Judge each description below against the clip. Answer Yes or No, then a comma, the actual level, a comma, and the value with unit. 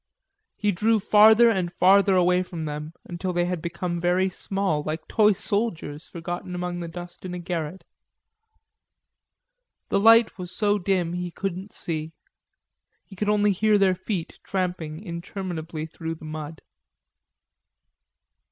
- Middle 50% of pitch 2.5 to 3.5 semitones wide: Yes, average, 2.9 semitones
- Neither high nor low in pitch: Yes, medium, 180 Hz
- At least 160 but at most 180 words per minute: No, average, 140 wpm